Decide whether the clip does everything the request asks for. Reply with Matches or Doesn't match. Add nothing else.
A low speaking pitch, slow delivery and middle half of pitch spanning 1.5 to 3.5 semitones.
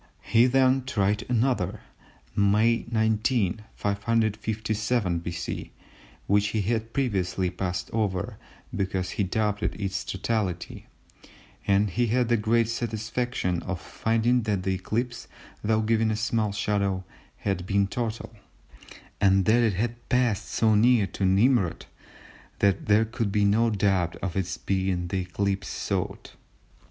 Matches